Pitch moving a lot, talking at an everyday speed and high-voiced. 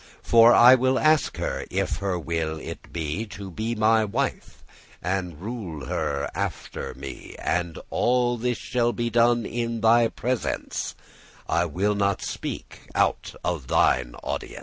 No: wide, 5.7 semitones; average, 150 wpm; low, 110 Hz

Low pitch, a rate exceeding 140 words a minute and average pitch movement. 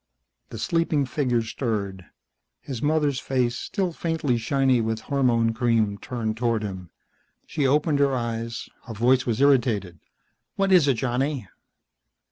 No: low, 125 Hz; slow, 135 wpm; average, 3.9 semitones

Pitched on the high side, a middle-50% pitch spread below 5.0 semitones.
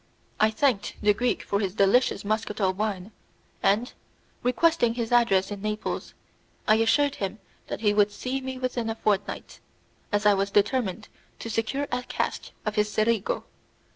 Yes: high, 215 Hz; average, 3.0 semitones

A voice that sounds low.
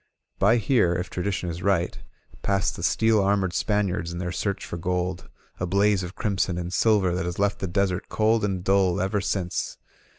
Yes: very low, 95 Hz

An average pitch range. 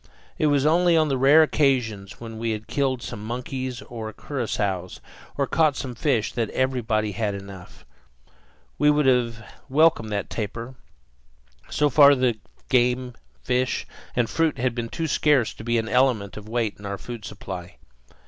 Yes: average, 3.9 semitones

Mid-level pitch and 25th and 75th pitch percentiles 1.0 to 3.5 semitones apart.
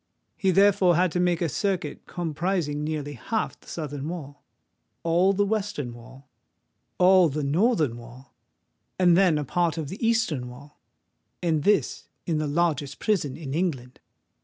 No: medium, 160 Hz; average, 4.4 semitones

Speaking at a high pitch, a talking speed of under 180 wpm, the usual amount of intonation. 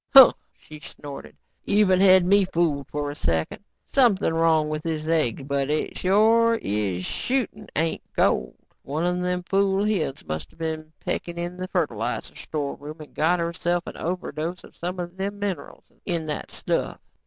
No: medium, 170 Hz; average, 165 wpm; average, 3.8 semitones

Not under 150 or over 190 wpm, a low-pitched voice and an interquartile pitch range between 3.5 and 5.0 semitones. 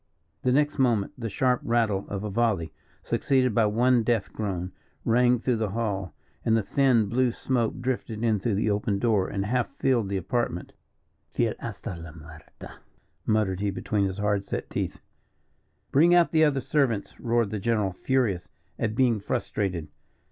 Yes: average, 170 wpm; low, 110 Hz; average, 3.8 semitones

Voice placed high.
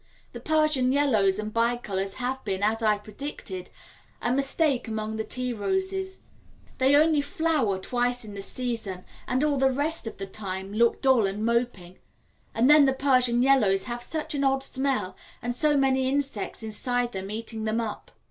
Yes: high, 245 Hz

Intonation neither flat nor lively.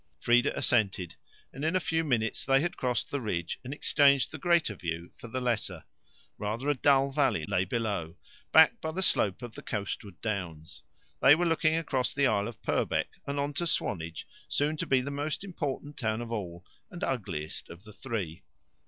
No: wide, 6.3 semitones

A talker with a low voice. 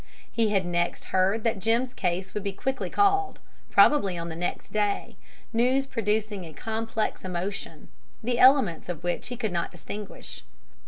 No: high, 210 Hz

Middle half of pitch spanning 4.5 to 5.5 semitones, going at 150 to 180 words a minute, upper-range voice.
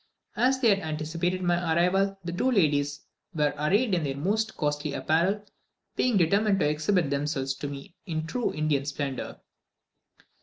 No: average, 5.0 semitones; average, 155 wpm; medium, 165 Hz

